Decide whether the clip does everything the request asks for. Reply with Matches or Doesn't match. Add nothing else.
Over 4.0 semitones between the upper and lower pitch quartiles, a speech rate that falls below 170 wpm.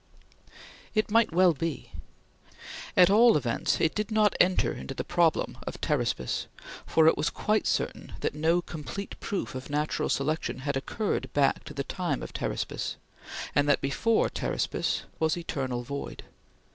Matches